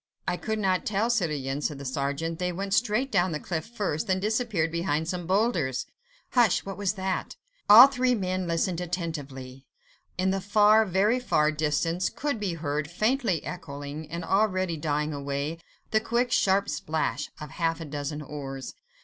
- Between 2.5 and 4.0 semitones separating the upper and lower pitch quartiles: No, average, 5.3 semitones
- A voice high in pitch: No, medium, 175 Hz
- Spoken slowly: No, average, 165 wpm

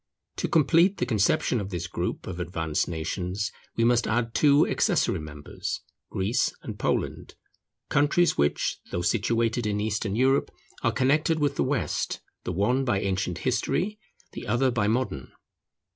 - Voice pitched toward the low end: Yes, low, 115 Hz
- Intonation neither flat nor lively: No, wide, 6.0 semitones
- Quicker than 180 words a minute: No, average, 150 wpm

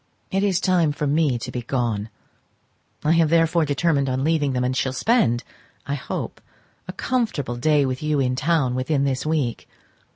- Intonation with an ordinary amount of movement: Yes, average, 4.2 semitones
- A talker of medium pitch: Yes, medium, 145 Hz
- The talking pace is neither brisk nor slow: Yes, average, 175 wpm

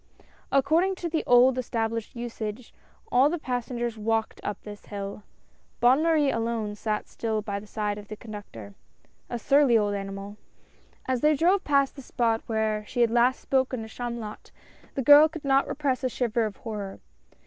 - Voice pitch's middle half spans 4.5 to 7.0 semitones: No, average, 4.1 semitones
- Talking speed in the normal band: Yes, average, 175 wpm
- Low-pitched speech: No, high, 235 Hz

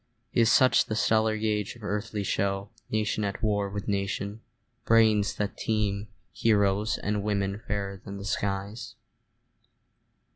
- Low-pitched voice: Yes, low, 105 Hz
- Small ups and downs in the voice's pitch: Yes, narrow, 1.5 semitones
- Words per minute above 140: No, slow, 135 wpm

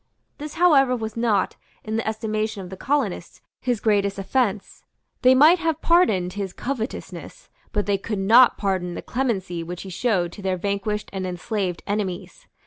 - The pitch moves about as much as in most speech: Yes, average, 4.5 semitones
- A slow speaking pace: No, average, 165 wpm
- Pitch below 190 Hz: No, high, 210 Hz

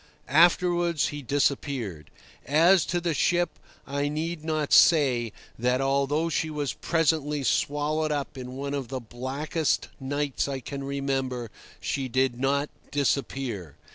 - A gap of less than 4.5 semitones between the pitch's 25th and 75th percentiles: Yes, average, 2.7 semitones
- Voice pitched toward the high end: No, medium, 140 Hz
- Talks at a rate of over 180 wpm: No, slow, 135 wpm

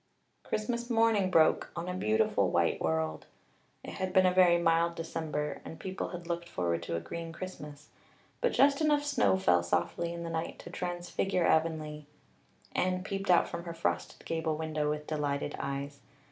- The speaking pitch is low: No, medium, 170 Hz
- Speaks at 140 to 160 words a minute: No, average, 175 wpm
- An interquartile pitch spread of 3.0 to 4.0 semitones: Yes, average, 3.6 semitones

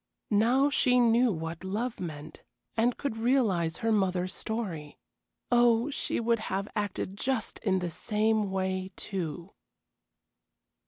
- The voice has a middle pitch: No, high, 210 Hz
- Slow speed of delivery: Yes, slow, 125 wpm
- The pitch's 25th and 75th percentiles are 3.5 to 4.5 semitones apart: Yes, average, 4.1 semitones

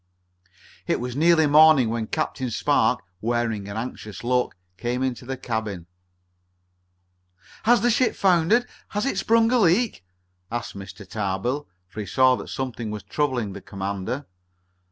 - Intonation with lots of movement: Yes, wide, 6.6 semitones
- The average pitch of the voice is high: No, low, 125 Hz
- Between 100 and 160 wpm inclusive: Yes, average, 145 wpm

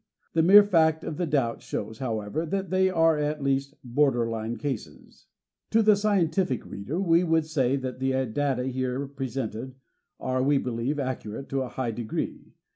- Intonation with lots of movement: No, average, 4.4 semitones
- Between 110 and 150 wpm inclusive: No, average, 185 wpm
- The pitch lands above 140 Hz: No, low, 135 Hz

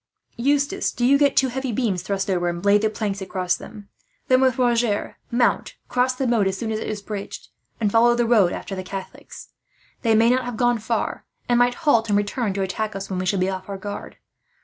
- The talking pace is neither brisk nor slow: No, fast, 230 wpm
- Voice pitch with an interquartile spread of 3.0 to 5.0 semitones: Yes, average, 3.7 semitones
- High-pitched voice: Yes, high, 220 Hz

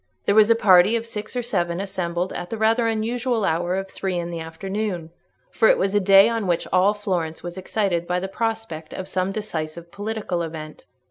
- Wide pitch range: No, average, 4.0 semitones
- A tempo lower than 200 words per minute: No, fast, 205 wpm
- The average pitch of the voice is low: No, high, 190 Hz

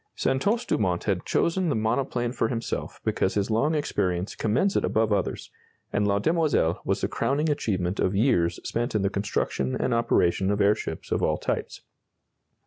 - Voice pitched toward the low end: Yes, low, 110 Hz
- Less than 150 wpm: No, average, 170 wpm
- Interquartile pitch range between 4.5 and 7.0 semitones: Yes, wide, 5.5 semitones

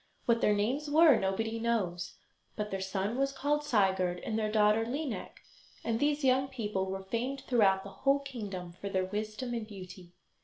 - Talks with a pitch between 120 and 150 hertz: No, high, 220 Hz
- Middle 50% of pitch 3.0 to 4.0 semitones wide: No, average, 5.3 semitones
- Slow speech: No, average, 180 wpm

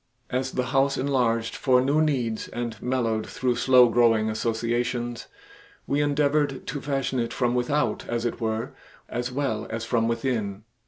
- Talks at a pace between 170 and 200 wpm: No, average, 155 wpm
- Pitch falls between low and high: No, low, 120 Hz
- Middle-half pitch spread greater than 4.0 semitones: No, average, 2.7 semitones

